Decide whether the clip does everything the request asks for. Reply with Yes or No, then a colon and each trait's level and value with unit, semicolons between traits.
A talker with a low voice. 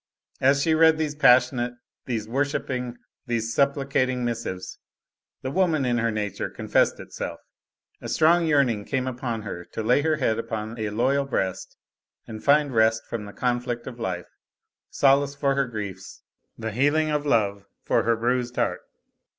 Yes: low, 125 Hz